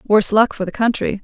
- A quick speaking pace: Yes, fast, 245 wpm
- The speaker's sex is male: No, female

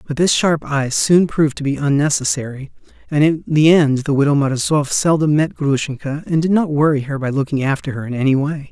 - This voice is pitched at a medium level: Yes, medium, 145 Hz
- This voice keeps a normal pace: No, fast, 215 wpm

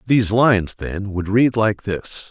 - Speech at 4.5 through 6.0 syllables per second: No, 4.3 syllables/s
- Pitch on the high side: No, low, 105 Hz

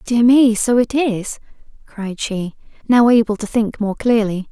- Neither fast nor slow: Yes, average, 175 wpm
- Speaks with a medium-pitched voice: No, high, 225 Hz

